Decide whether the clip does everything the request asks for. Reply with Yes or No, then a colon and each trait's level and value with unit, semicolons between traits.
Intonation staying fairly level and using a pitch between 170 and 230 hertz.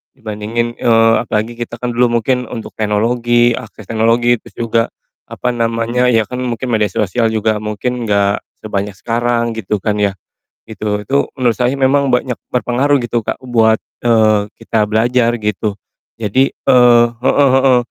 No: narrow, 2.2 semitones; low, 115 Hz